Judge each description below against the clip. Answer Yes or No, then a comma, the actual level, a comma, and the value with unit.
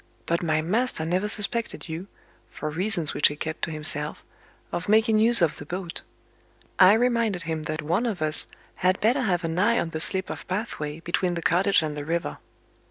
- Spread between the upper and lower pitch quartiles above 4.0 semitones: Yes, average, 4.8 semitones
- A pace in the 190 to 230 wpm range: Yes, average, 195 wpm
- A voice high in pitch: No, medium, 175 Hz